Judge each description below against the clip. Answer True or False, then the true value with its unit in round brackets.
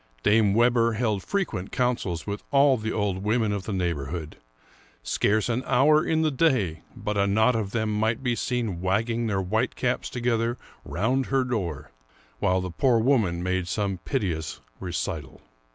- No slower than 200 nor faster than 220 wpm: False (165 wpm)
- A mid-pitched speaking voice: False (110 Hz)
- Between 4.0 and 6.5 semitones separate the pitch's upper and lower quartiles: True (4.8 semitones)